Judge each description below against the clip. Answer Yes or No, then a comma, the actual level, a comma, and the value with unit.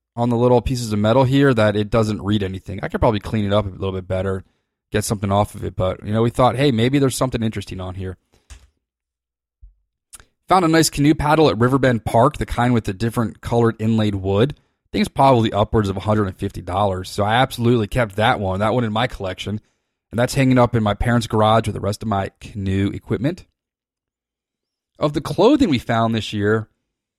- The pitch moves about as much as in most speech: Yes, average, 3.6 semitones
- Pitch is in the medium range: No, low, 110 Hz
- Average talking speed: No, fast, 210 wpm